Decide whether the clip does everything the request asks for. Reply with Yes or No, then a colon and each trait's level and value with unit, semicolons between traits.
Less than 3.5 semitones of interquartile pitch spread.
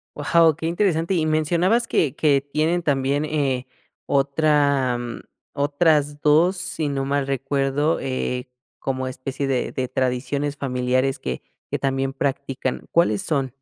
Yes: narrow, 2.6 semitones